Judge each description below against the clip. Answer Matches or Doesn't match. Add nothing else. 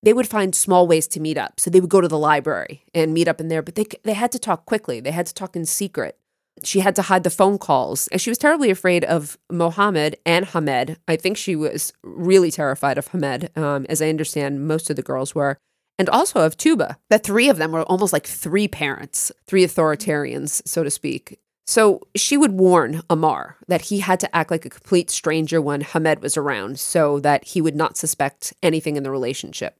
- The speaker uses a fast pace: Matches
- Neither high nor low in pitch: Matches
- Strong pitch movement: Doesn't match